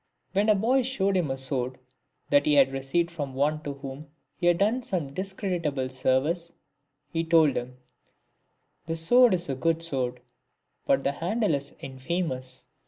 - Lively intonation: Yes, wide, 5.8 semitones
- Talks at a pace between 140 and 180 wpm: Yes, average, 170 wpm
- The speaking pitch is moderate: Yes, medium, 165 Hz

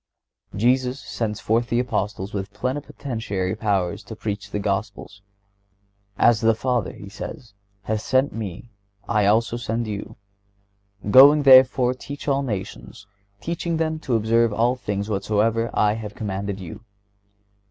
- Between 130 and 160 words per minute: Yes, average, 140 wpm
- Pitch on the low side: Yes, low, 110 Hz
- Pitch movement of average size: Yes, average, 3.6 semitones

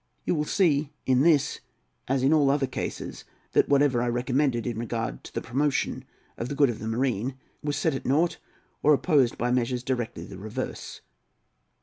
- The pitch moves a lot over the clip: No, average, 3.3 semitones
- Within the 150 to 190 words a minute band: Yes, average, 185 wpm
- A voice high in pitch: No, low, 130 Hz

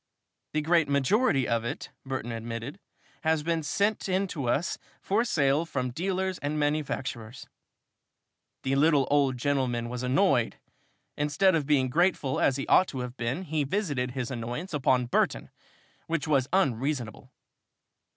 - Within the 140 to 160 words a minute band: Yes, average, 145 wpm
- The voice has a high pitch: No, medium, 140 Hz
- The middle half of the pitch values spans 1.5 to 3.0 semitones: No, average, 4.7 semitones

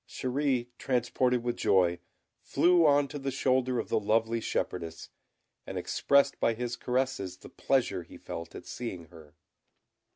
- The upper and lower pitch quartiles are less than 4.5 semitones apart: No, average, 5.3 semitones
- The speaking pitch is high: No, low, 120 Hz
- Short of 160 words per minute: Yes, average, 150 wpm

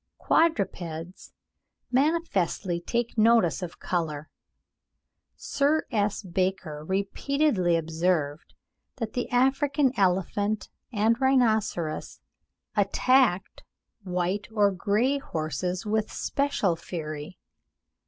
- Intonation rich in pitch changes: Yes, wide, 5.9 semitones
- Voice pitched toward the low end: No, high, 200 Hz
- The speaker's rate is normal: No, slow, 85 wpm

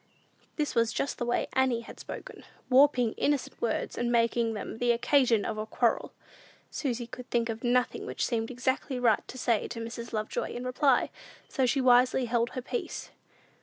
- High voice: Yes, high, 240 Hz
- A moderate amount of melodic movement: No, narrow, 1.7 semitones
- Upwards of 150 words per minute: Yes, average, 180 wpm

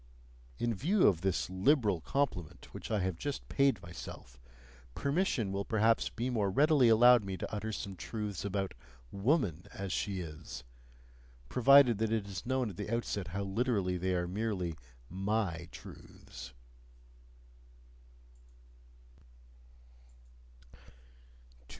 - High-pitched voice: No, low, 100 Hz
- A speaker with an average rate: No, slow, 120 wpm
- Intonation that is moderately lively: Yes, average, 4.4 semitones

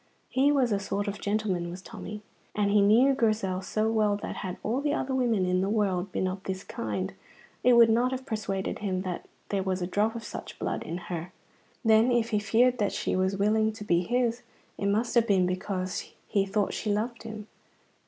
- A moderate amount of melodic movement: Yes, average, 3.3 semitones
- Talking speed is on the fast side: Yes, fast, 210 wpm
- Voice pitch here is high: Yes, high, 210 Hz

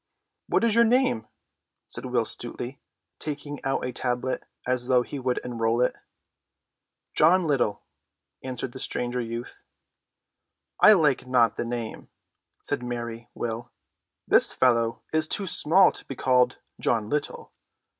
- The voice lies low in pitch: Yes, low, 125 Hz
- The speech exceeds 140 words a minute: No, slow, 135 wpm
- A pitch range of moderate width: Yes, average, 3.4 semitones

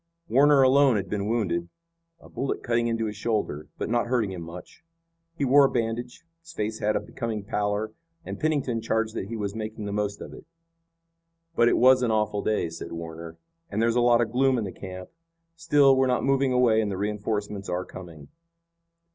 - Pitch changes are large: No, average, 3.5 semitones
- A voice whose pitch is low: Yes, low, 110 Hz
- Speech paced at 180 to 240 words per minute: Yes, average, 200 wpm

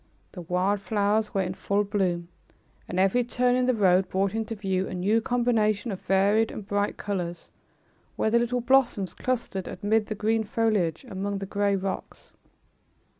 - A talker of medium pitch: No, high, 205 Hz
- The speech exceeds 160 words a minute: Yes, average, 170 wpm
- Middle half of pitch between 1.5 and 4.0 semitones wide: Yes, average, 2.8 semitones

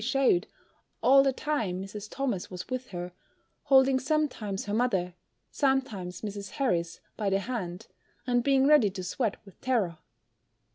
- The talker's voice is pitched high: Yes, high, 220 Hz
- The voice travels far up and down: Yes, wide, 6.0 semitones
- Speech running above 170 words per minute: No, average, 145 wpm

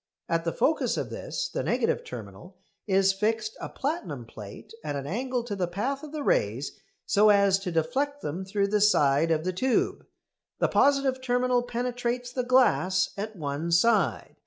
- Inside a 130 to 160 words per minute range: No, average, 175 wpm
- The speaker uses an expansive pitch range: Yes, wide, 6.5 semitones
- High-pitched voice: Yes, high, 210 Hz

